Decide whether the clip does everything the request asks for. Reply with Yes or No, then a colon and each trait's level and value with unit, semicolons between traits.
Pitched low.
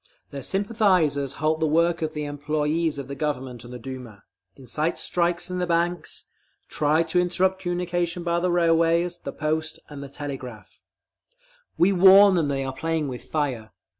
No: medium, 160 Hz